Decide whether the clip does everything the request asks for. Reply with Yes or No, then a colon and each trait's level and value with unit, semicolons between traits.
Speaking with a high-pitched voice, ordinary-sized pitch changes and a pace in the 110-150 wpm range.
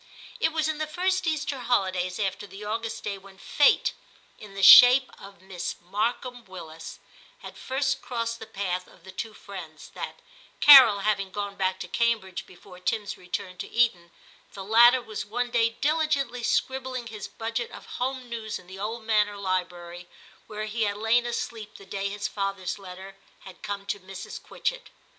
No: high, 210 Hz; average, 4.0 semitones; average, 175 wpm